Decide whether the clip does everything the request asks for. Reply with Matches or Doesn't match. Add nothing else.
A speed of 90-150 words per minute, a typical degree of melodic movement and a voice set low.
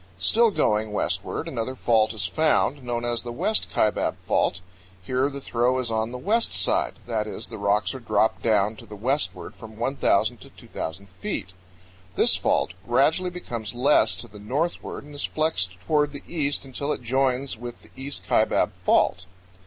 Doesn't match